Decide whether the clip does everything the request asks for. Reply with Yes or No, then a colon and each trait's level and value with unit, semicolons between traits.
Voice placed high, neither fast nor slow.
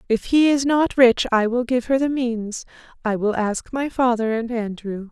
No: high, 240 Hz; fast, 210 wpm